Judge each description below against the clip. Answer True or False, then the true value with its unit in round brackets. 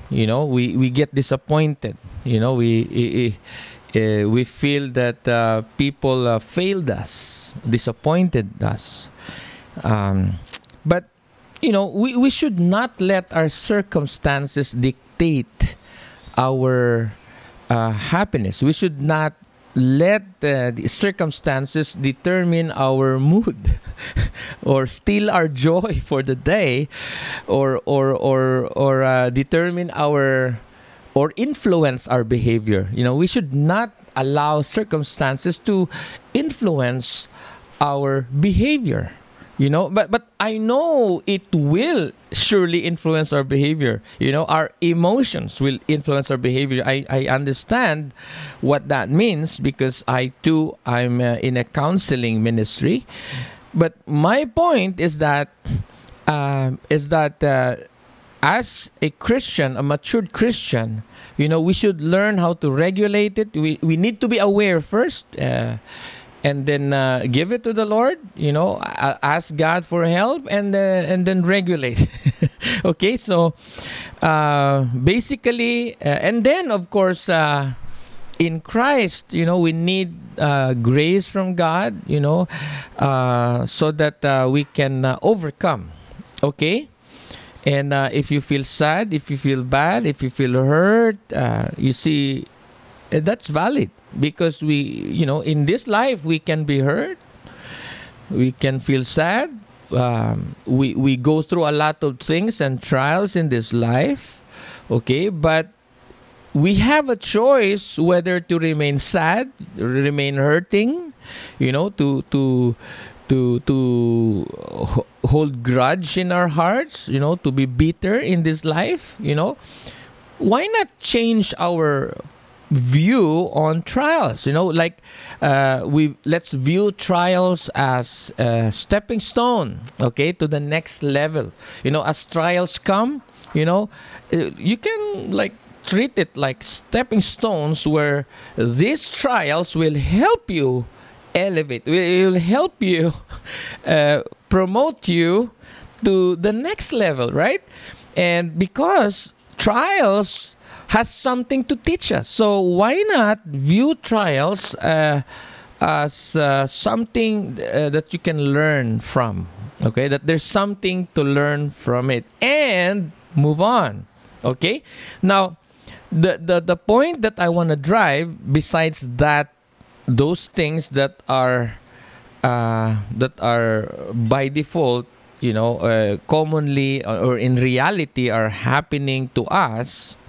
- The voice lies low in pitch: False (150 Hz)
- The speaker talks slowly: True (130 wpm)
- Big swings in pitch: True (5.9 semitones)